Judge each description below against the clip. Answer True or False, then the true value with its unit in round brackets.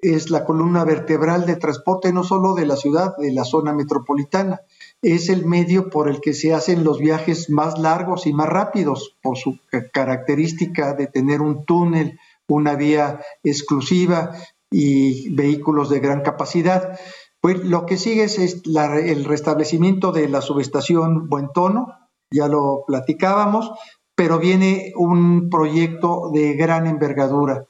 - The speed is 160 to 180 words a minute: False (145 wpm)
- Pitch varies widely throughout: False (3.4 semitones)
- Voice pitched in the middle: True (160 Hz)